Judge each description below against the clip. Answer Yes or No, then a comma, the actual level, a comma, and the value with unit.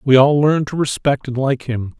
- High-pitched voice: No, low, 135 Hz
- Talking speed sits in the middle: No, fast, 240 wpm